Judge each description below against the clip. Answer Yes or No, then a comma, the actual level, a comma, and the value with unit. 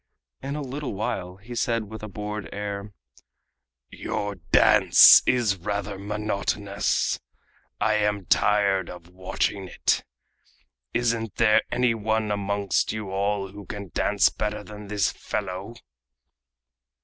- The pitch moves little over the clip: Yes, narrow, 1.6 semitones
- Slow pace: Yes, slow, 125 wpm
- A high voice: No, low, 105 Hz